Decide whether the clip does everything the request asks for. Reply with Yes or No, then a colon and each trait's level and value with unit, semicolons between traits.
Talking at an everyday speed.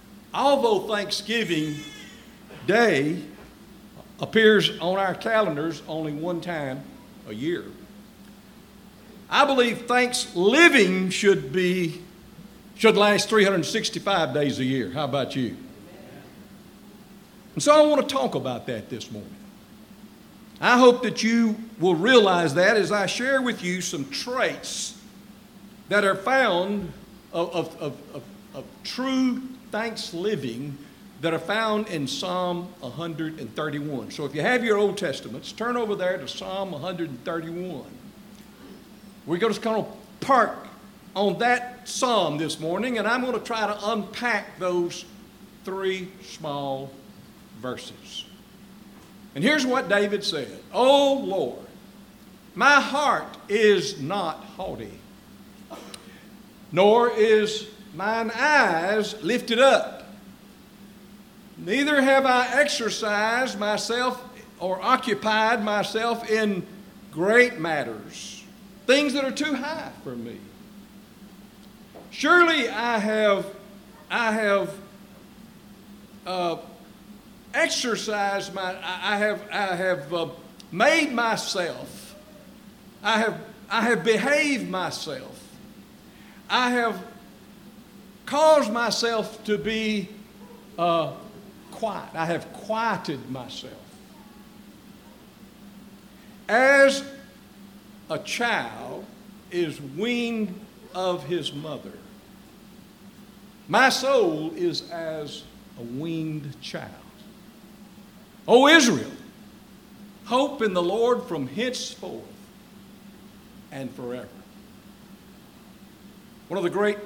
No: slow, 105 wpm